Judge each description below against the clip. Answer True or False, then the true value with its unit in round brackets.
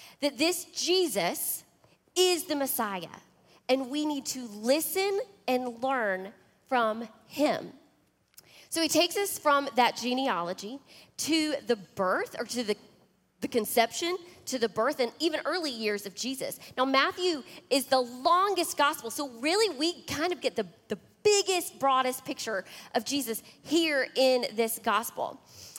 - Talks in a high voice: True (270 Hz)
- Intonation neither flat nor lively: False (5.8 semitones)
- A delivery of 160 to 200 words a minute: False (145 wpm)